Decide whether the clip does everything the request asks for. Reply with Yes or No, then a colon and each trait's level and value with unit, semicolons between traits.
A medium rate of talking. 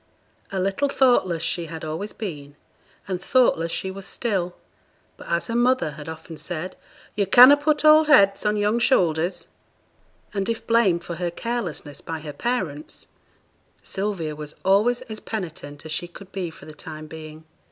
Yes: average, 165 wpm